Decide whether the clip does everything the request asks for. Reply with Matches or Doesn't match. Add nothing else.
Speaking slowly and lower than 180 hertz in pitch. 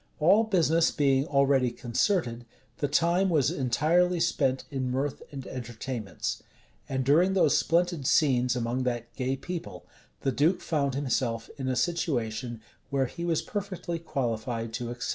Doesn't match